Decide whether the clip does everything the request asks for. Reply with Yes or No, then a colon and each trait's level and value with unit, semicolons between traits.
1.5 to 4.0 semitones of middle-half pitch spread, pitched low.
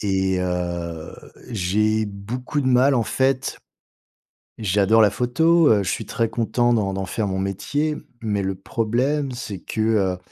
No: average, 4.5 semitones; low, 110 Hz